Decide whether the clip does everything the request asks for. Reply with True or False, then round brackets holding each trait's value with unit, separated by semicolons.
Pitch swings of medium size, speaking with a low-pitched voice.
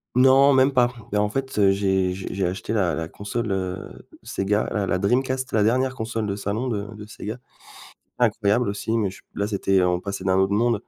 True (3.6 semitones; 105 Hz)